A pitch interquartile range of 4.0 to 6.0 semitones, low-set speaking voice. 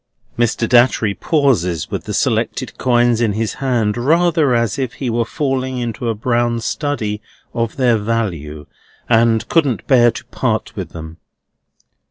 No: average, 2.9 semitones; low, 120 Hz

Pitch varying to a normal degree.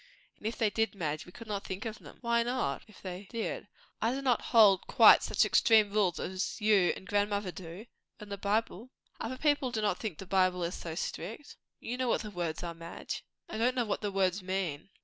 Yes: average, 3.6 semitones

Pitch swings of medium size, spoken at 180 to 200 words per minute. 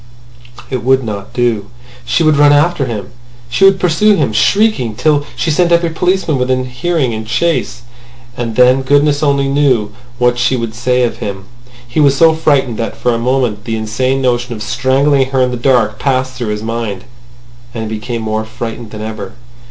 Yes: average, 4.1 semitones; average, 190 wpm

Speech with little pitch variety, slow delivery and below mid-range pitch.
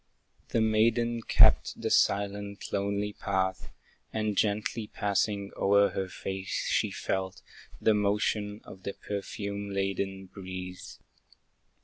Yes: narrow, 1.3 semitones; slow, 110 wpm; low, 100 Hz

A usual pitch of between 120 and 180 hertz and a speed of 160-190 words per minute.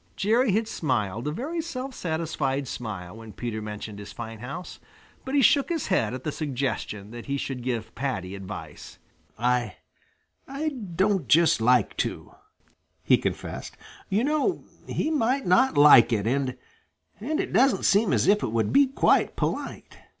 Yes: medium, 140 Hz; average, 165 wpm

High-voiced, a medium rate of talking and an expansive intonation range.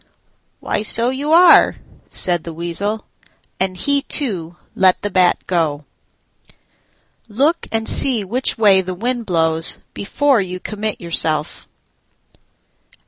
No: high, 200 Hz; slow, 120 wpm; wide, 5.7 semitones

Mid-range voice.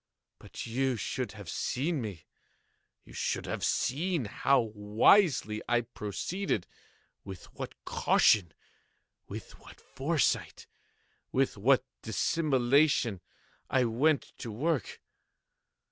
No: low, 120 Hz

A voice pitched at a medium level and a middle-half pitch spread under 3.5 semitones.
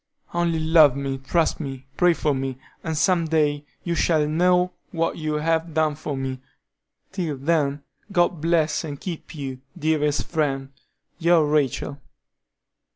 Yes: medium, 155 Hz; average, 2.8 semitones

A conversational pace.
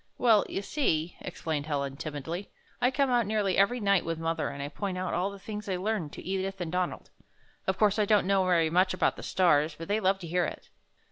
No: fast, 230 wpm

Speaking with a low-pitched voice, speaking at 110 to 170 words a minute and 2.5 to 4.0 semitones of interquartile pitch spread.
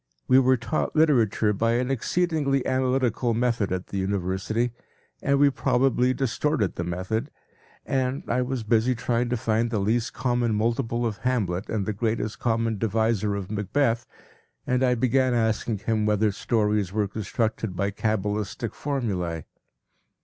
Yes: low, 115 Hz; average, 150 wpm; average, 3.2 semitones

